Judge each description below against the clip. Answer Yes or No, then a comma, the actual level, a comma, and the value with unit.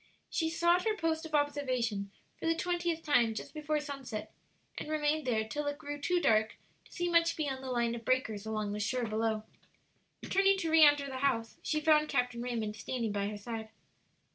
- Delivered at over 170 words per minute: Yes, average, 195 wpm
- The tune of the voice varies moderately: No, wide, 5.7 semitones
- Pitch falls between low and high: No, very high, 275 Hz